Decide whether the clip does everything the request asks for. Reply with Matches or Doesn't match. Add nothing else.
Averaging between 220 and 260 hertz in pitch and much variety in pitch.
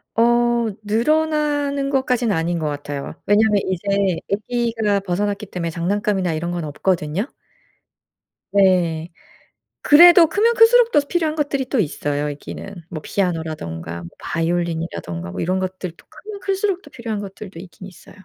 Doesn't match